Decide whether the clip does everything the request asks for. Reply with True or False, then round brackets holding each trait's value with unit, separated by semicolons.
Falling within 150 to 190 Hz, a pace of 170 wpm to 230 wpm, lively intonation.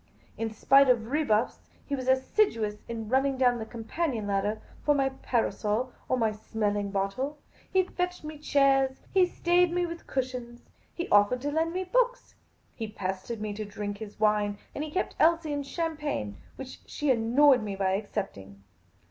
False (250 Hz; 175 wpm; 5.9 semitones)